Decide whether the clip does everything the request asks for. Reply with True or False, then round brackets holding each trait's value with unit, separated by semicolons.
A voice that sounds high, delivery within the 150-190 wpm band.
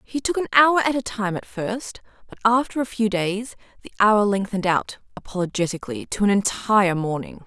True (210 Hz; 185 wpm)